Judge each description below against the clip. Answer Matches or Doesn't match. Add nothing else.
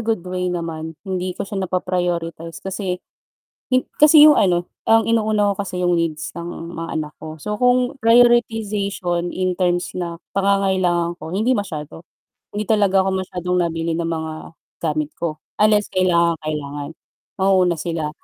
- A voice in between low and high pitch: Matches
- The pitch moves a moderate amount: Matches